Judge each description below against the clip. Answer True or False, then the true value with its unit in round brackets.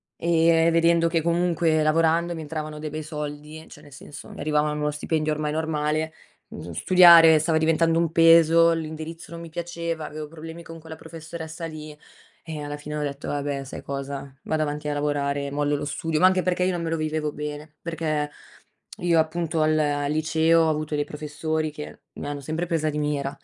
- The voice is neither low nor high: True (155 Hz)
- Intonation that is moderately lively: False (1.8 semitones)